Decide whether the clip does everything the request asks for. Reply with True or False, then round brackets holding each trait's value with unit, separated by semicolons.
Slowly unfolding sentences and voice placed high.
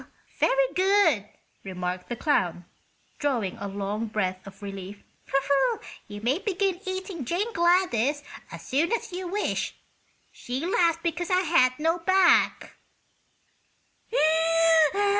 True (115 wpm; 300 Hz)